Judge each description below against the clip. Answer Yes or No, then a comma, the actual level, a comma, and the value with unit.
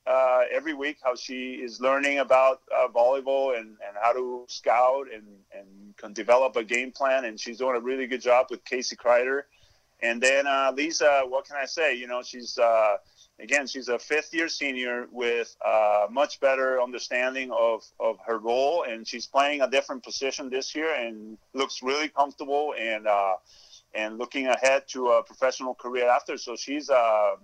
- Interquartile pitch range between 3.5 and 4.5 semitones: No, average, 2.7 semitones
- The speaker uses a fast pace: No, average, 185 wpm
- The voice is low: Yes, low, 130 Hz